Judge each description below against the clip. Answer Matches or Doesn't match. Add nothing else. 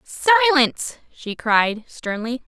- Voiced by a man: Doesn't match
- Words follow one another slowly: Matches